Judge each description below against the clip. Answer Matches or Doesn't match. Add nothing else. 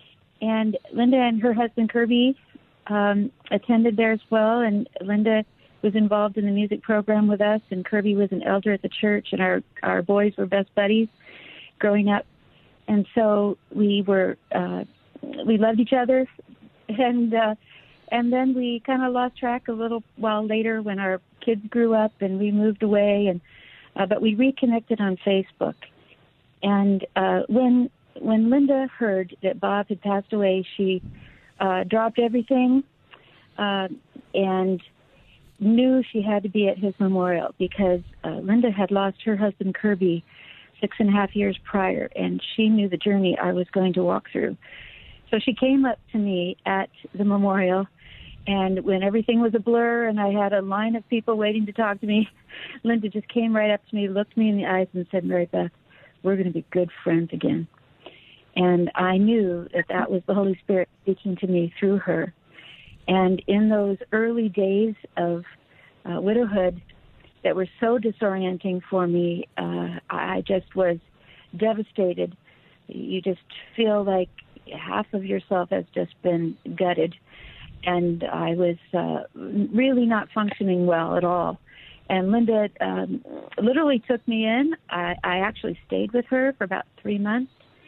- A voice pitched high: Matches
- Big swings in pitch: Doesn't match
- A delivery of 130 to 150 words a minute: Doesn't match